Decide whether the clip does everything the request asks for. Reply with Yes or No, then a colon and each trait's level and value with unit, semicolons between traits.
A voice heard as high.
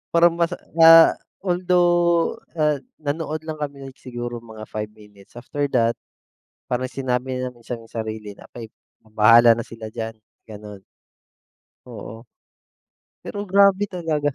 No: low, 130 Hz